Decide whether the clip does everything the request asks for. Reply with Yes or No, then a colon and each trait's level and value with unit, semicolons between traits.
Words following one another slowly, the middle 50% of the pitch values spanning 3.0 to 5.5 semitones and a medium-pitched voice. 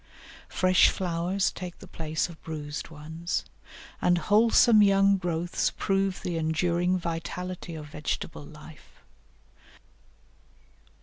No: slow, 105 wpm; narrow, 2.5 semitones; medium, 175 Hz